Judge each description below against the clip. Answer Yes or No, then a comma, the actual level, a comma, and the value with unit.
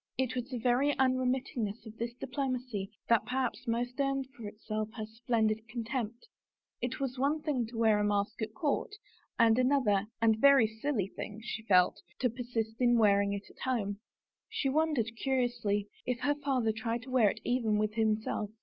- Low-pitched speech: No, high, 235 Hz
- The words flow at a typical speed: Yes, average, 185 wpm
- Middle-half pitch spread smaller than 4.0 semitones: Yes, average, 3.0 semitones